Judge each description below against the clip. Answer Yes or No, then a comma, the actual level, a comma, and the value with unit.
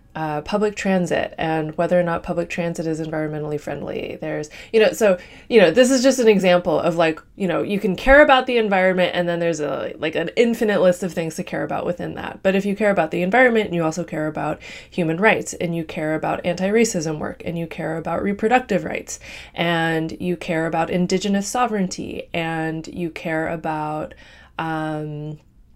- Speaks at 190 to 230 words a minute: Yes, average, 195 wpm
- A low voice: No, medium, 170 Hz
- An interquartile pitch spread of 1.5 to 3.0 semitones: No, average, 3.8 semitones